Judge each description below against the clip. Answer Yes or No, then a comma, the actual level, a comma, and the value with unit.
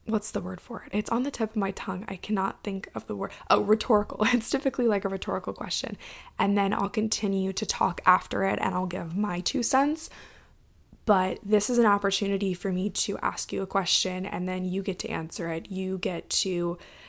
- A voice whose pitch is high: Yes, high, 200 Hz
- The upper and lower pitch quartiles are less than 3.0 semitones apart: Yes, narrow, 2.4 semitones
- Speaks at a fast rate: Yes, fast, 220 wpm